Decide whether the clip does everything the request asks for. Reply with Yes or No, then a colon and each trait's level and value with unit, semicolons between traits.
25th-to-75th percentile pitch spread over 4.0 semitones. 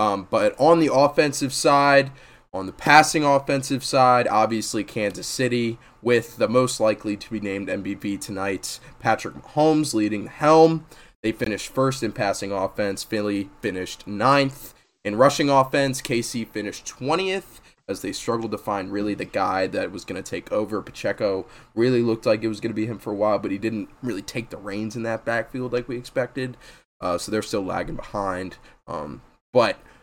Yes: average, 4.6 semitones